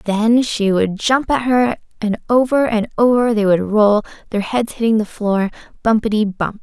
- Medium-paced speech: Yes, average, 180 wpm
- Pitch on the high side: Yes, high, 220 Hz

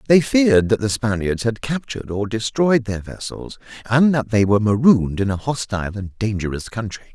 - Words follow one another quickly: No, average, 185 wpm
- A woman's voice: No, male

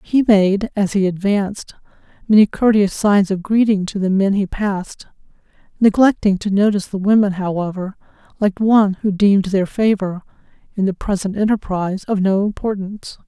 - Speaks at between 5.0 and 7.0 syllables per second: Yes, 5.3 syllables/s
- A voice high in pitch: Yes, high, 200 Hz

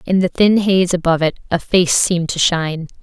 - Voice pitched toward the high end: No, medium, 175 Hz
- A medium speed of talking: No, fast, 220 wpm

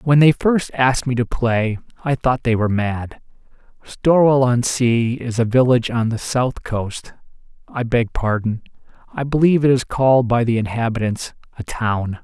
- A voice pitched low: Yes, low, 120 Hz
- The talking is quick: No, average, 165 wpm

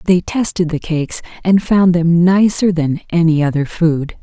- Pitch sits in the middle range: Yes, medium, 170 Hz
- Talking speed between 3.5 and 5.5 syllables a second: Yes, 4.5 syllables/s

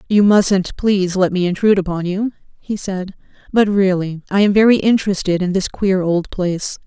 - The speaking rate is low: No, average, 185 wpm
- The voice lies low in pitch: No, high, 190 Hz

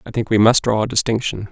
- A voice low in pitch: Yes, low, 110 Hz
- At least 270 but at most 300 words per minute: Yes, fast, 275 wpm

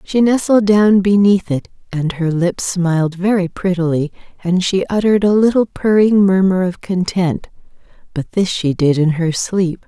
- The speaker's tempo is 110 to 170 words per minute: Yes, average, 165 wpm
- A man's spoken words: No, female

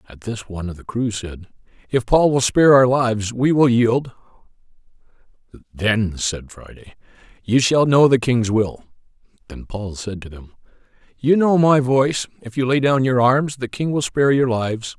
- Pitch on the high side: No, low, 120 Hz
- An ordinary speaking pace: Yes, average, 185 wpm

